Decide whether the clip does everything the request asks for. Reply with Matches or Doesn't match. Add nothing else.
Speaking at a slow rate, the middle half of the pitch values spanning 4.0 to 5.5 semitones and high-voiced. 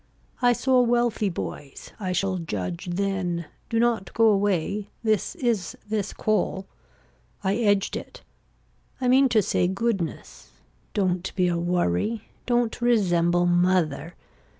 Matches